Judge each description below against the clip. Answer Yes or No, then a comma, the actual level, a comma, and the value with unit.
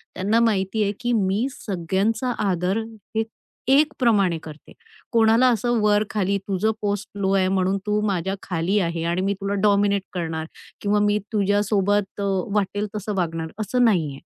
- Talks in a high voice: Yes, high, 200 Hz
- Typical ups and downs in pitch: No, narrow, 2.2 semitones